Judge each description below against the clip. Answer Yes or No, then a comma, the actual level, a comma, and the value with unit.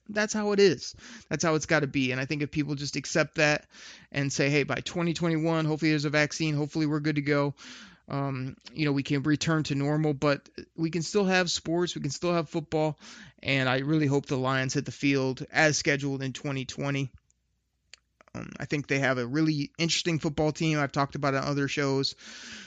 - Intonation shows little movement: Yes, narrow, 2.3 semitones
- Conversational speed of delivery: No, fast, 210 wpm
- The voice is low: No, medium, 150 Hz